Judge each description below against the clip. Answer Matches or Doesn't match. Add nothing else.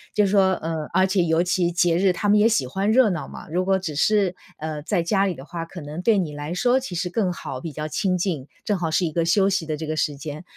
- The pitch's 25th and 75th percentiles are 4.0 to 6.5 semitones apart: Doesn't match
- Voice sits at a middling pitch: Matches